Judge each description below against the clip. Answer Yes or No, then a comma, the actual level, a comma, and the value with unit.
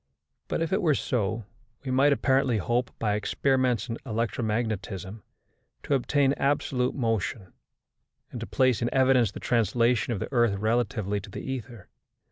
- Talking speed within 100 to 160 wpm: Yes, average, 150 wpm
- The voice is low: Yes, low, 120 Hz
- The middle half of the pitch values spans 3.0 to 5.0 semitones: Yes, average, 3.5 semitones